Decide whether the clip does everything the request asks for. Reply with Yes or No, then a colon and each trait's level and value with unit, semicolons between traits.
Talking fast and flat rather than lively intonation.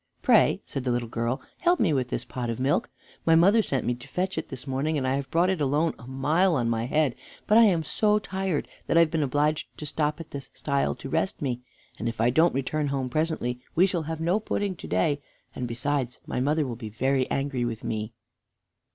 No: fast, 240 wpm; average, 4.6 semitones